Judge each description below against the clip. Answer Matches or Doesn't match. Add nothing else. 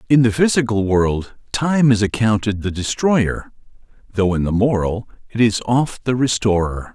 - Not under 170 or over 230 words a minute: Doesn't match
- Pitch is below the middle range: Matches